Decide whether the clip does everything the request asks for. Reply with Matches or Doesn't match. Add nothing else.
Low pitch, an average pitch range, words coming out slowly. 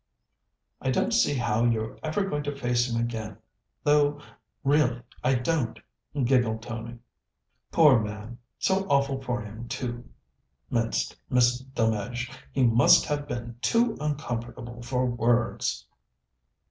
Matches